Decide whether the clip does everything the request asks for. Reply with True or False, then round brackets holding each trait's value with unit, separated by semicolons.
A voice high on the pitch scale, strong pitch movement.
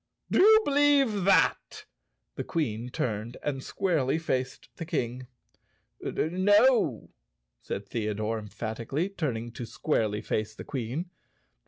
False (130 Hz; 8.7 semitones)